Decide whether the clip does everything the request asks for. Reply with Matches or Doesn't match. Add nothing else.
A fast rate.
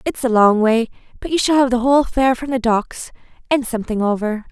Matches